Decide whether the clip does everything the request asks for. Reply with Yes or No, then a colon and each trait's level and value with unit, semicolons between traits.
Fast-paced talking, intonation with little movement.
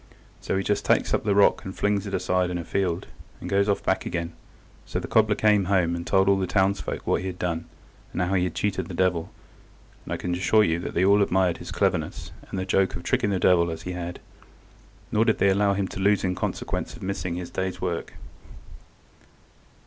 Yes: fast, 225 wpm; narrow, 2.0 semitones